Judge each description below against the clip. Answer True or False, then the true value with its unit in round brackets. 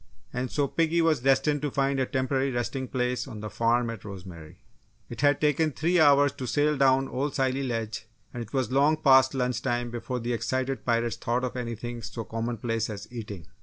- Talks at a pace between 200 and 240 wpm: True (205 wpm)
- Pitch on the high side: False (125 Hz)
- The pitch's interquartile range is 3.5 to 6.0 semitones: False (2.9 semitones)